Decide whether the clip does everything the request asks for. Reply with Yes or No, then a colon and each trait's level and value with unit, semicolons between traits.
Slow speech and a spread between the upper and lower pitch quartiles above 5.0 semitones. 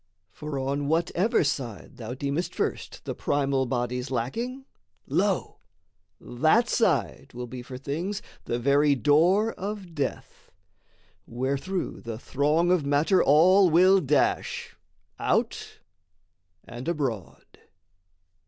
Yes: slow, 110 wpm; wide, 5.6 semitones